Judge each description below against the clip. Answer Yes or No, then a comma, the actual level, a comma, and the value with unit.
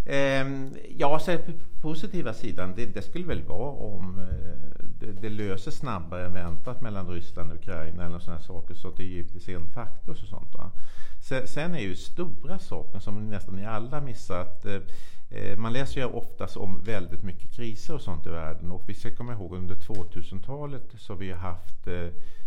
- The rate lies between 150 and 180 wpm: Yes, average, 170 wpm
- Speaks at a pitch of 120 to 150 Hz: No, low, 100 Hz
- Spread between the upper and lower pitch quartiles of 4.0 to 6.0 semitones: Yes, average, 5.1 semitones